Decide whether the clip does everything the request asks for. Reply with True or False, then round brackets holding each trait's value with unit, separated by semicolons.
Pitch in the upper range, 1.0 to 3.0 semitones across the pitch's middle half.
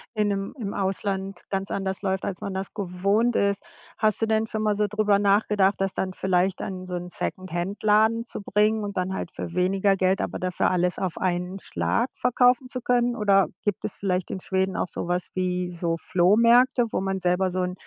True (195 Hz; 2.4 semitones)